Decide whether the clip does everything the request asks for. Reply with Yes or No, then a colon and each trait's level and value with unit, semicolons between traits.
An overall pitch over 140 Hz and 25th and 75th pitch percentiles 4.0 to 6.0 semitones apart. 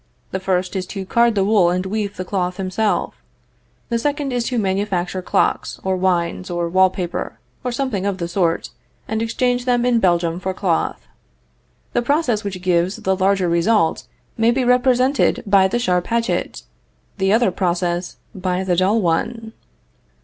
Yes: high, 190 Hz; average, 4.3 semitones